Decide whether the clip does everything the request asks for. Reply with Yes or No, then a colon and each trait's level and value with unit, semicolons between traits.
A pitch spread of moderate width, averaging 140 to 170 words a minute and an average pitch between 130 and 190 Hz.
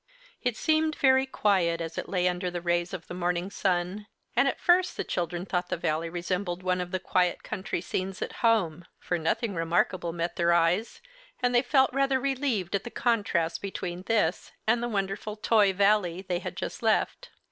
No: average, 4.5 semitones; average, 190 wpm; medium, 185 Hz